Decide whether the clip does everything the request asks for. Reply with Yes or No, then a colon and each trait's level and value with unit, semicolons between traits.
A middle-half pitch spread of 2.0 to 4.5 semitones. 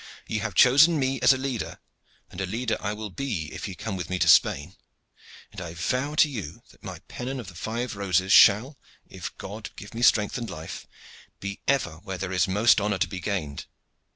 No: average, 5.2 semitones